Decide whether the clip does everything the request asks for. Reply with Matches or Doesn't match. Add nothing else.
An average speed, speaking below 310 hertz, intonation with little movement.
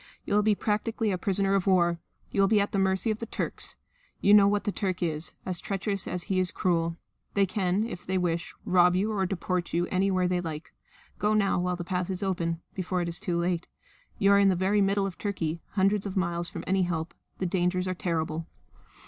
Doesn't match